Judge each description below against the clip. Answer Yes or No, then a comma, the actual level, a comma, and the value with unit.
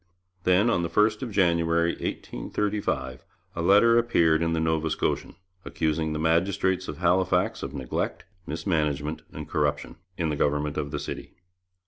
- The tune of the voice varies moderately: Yes, average, 3.7 semitones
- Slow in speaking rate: No, average, 150 wpm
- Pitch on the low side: Yes, very low, 80 Hz